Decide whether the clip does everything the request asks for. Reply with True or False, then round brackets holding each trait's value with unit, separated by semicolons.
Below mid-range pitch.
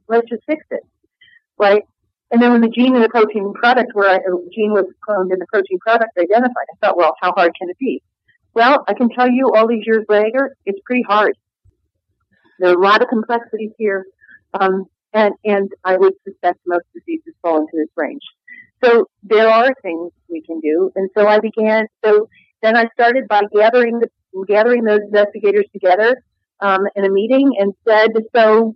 False (215 Hz)